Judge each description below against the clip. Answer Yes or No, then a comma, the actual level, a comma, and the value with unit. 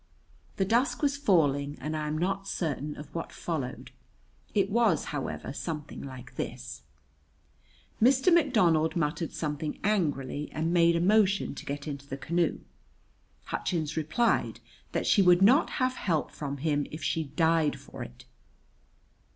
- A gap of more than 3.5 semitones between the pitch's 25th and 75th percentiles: Yes, average, 5.0 semitones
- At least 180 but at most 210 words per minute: No, average, 145 wpm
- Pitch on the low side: No, medium, 160 Hz